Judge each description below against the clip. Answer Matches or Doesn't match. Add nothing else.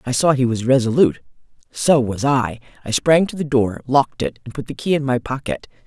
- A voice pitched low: Matches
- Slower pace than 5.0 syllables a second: Doesn't match